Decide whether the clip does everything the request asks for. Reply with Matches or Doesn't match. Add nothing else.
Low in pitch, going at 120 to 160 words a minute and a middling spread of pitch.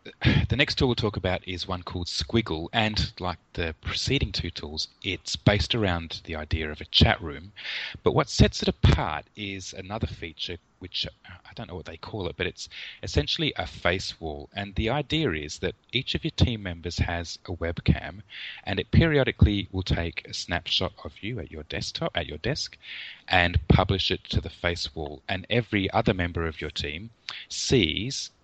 Doesn't match